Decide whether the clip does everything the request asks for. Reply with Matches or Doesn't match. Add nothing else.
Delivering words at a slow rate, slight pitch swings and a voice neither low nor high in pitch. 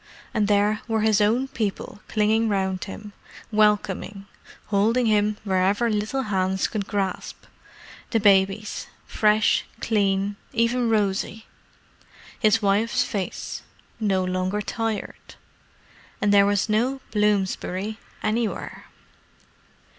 Doesn't match